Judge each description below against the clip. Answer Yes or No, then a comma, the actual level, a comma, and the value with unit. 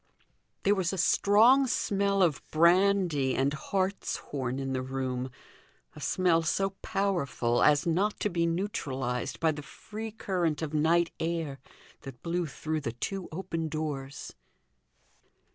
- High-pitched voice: No, medium, 165 Hz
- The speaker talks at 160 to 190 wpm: No, slow, 135 wpm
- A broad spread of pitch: Yes, wide, 5.7 semitones